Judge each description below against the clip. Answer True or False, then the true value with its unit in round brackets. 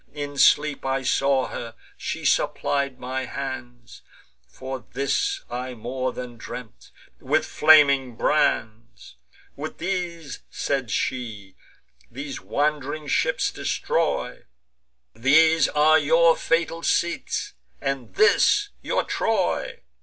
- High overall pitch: False (140 Hz)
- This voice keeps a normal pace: False (105 wpm)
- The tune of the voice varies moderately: True (3.8 semitones)